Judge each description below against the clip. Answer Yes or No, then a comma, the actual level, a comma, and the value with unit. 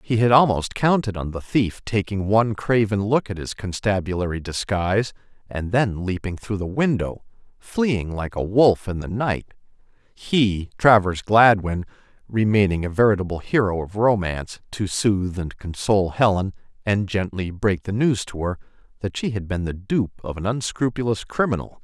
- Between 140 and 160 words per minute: Yes, average, 155 wpm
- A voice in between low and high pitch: No, low, 100 Hz